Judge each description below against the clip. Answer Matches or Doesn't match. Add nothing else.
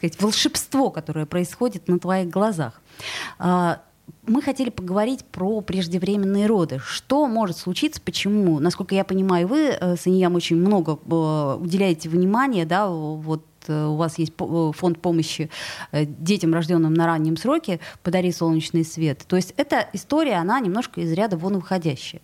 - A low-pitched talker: Doesn't match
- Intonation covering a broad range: Doesn't match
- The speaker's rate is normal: Matches